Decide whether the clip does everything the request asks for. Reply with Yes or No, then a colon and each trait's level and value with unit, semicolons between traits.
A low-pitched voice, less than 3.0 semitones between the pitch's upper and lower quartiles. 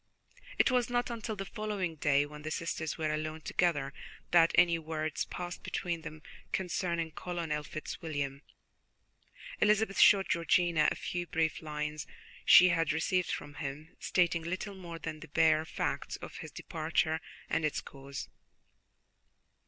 No: medium, 165 Hz; narrow, 2.6 semitones